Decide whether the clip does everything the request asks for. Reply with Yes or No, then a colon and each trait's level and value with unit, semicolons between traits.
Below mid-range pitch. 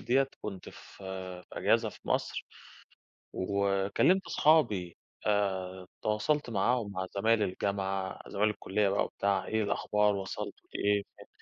Yes: low, 100 Hz